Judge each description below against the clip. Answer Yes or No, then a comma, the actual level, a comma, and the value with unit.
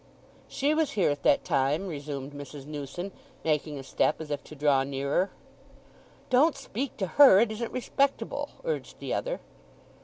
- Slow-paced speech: No, average, 155 wpm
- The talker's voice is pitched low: No, medium, 155 Hz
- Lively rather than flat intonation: Yes, wide, 8.9 semitones